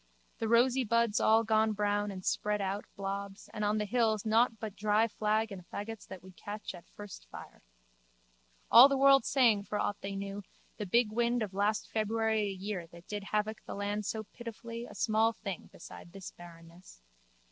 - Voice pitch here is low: No, high, 210 Hz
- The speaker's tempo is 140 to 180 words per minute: No, average, 190 wpm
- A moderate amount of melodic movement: No, narrow, 2.1 semitones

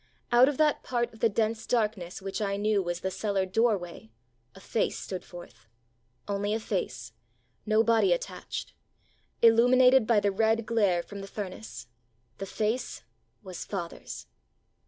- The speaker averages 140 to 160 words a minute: Yes, average, 155 wpm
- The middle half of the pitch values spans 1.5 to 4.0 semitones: Yes, average, 3.5 semitones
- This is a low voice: No, high, 210 Hz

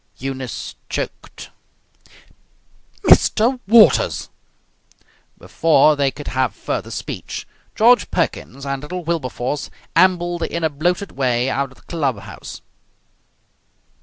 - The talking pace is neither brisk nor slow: No, slow, 105 wpm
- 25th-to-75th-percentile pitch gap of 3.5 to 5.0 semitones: Yes, average, 4.7 semitones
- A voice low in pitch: No, medium, 150 Hz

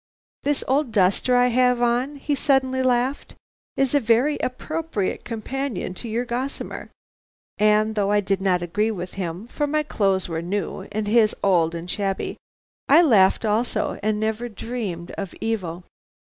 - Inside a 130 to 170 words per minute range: Yes, average, 160 wpm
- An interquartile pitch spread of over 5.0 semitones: No, average, 4.6 semitones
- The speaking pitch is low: No, high, 220 Hz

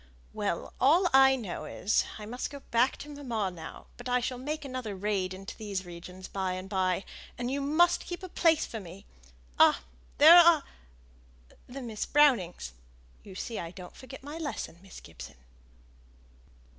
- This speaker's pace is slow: No, average, 165 wpm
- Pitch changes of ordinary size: No, wide, 7.1 semitones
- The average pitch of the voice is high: Yes, high, 235 Hz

